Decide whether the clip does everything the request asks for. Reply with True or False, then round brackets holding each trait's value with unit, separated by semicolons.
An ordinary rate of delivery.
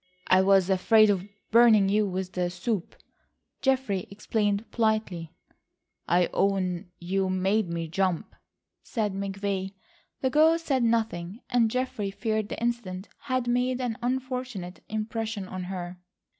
False (130 wpm)